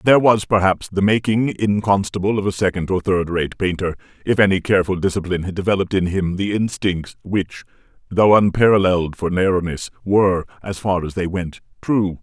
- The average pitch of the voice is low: Yes, very low, 95 Hz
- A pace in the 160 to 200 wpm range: Yes, average, 175 wpm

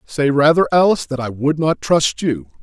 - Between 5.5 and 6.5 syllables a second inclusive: No, 5.0 syllables/s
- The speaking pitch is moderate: Yes, medium, 145 Hz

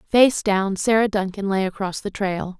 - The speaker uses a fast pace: No, average, 185 wpm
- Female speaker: Yes, female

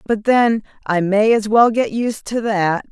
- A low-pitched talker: No, high, 215 Hz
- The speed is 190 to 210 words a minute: Yes, fast, 205 wpm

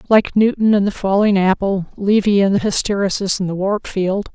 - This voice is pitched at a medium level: No, high, 200 Hz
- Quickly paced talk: No, average, 195 wpm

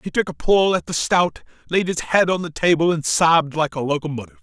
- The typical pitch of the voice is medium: Yes, medium, 160 Hz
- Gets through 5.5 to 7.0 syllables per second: Yes, 5.9 syllables/s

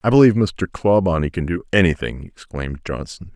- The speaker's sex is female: No, male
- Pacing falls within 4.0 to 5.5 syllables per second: No, 5.7 syllables/s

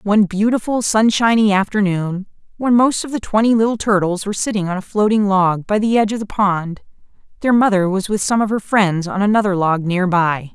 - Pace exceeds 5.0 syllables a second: Yes, 5.5 syllables/s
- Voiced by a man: No, female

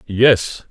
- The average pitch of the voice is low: Yes, low, 115 Hz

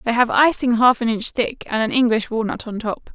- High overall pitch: Yes, high, 235 Hz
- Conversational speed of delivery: No, fast, 250 wpm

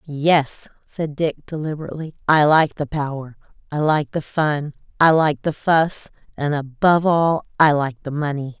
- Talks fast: No, average, 160 wpm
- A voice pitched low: No, medium, 150 Hz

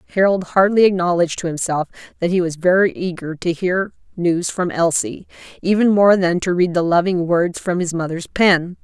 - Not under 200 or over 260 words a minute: No, average, 185 wpm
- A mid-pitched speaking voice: Yes, medium, 175 Hz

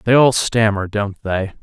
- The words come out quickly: No, average, 185 wpm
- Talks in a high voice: No, low, 105 Hz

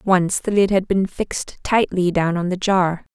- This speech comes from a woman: Yes, female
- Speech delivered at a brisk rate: Yes, fast, 210 wpm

